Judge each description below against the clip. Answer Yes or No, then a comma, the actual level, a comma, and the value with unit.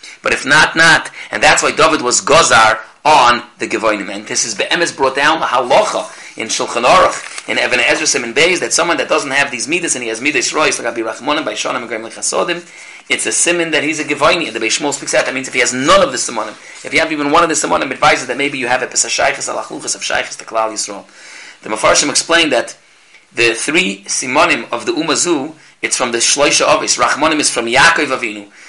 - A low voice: No, medium, 145 Hz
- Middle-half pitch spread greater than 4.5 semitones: Yes, average, 5.2 semitones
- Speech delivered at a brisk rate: Yes, fast, 220 wpm